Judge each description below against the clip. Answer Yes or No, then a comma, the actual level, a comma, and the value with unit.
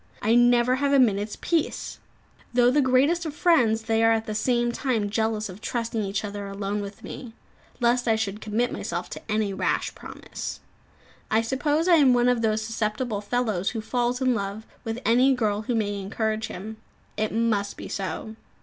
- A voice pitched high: Yes, high, 225 Hz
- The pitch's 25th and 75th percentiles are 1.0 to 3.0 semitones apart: Yes, average, 2.7 semitones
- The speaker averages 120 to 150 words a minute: No, average, 185 wpm